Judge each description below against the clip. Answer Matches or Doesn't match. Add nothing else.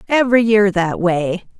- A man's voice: Doesn't match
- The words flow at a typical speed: Matches